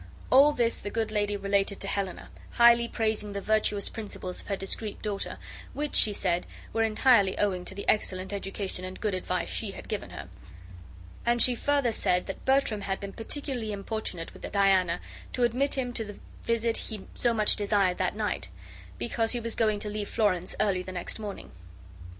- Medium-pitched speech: No, high, 210 Hz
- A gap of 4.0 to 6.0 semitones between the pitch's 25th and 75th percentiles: No, average, 2.8 semitones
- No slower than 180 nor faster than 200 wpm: Yes, average, 185 wpm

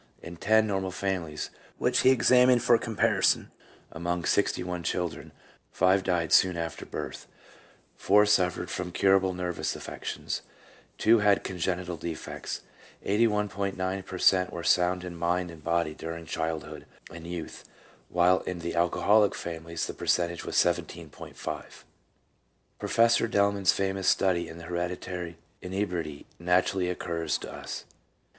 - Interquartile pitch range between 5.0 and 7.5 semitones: No, narrow, 2.4 semitones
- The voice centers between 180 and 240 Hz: No, very low, 90 Hz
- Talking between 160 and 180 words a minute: No, slow, 135 wpm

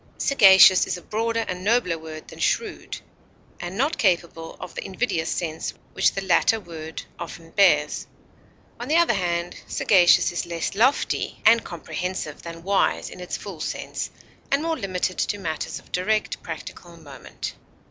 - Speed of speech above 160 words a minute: No, average, 155 wpm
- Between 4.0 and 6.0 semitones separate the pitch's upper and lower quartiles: Yes, average, 4.4 semitones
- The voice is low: No, medium, 185 Hz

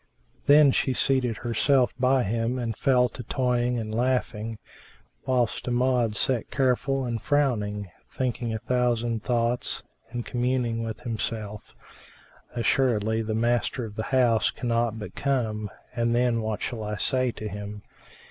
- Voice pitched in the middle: No, low, 120 Hz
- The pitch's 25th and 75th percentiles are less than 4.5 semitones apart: Yes, narrow, 2.4 semitones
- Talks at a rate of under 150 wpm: Yes, average, 140 wpm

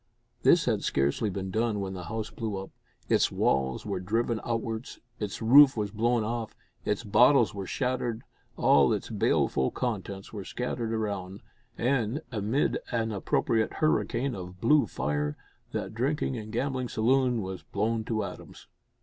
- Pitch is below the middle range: Yes, low, 110 Hz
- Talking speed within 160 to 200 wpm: No, average, 150 wpm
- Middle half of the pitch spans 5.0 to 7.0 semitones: No, average, 3.5 semitones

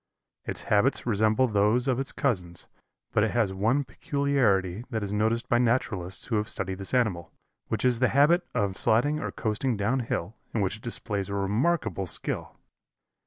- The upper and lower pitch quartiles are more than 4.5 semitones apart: No, average, 4.1 semitones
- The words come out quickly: No, average, 175 wpm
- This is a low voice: Yes, low, 110 Hz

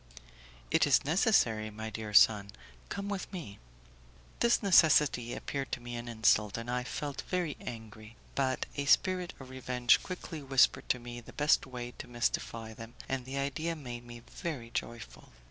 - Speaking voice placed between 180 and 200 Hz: No, low, 125 Hz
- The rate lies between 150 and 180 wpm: Yes, average, 165 wpm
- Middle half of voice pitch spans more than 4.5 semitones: No, average, 4.1 semitones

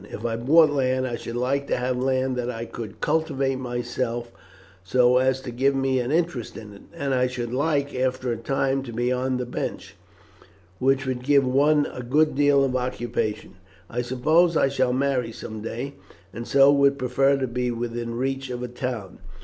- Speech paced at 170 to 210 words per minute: Yes, average, 195 wpm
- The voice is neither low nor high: No, low, 130 Hz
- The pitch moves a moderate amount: No, narrow, 2.2 semitones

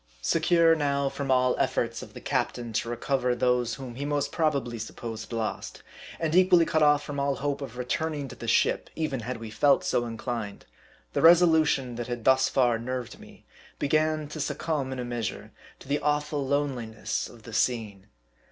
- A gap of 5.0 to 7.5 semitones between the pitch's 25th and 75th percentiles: No, average, 3.6 semitones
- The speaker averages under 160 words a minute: No, average, 185 wpm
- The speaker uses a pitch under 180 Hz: Yes, low, 135 Hz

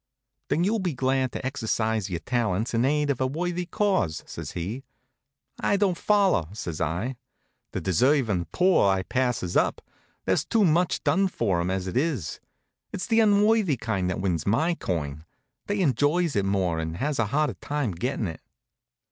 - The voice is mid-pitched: No, low, 125 Hz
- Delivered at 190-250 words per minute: No, average, 175 wpm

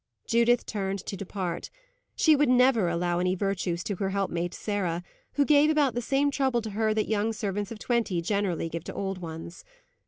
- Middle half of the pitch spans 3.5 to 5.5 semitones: Yes, average, 5.0 semitones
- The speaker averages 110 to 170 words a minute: No, average, 190 wpm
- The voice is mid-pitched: No, high, 205 Hz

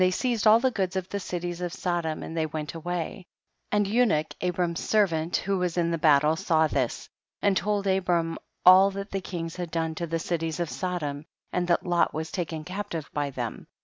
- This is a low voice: No, medium, 175 Hz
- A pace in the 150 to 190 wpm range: No, fast, 205 wpm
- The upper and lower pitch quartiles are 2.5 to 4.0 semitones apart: Yes, average, 2.9 semitones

